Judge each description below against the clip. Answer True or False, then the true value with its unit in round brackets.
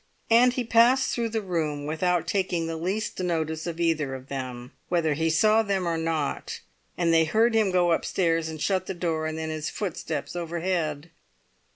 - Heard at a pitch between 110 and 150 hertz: False (170 Hz)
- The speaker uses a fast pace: False (185 wpm)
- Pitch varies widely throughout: False (3.1 semitones)